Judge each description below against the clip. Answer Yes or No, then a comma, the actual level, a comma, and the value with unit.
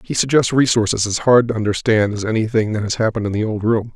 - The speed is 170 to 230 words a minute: No, fast, 245 wpm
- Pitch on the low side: Yes, low, 110 Hz